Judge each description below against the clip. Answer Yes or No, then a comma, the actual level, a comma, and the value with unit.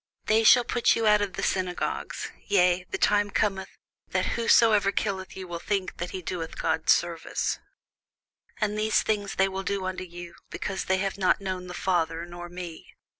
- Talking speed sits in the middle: Yes, average, 180 wpm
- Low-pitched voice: No, high, 190 Hz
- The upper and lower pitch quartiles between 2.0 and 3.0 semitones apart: Yes, narrow, 2.4 semitones